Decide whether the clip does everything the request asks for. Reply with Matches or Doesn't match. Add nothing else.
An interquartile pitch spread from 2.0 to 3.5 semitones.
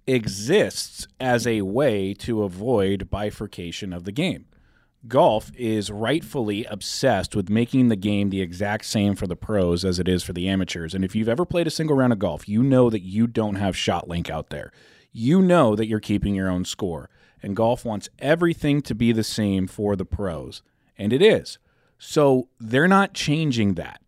Doesn't match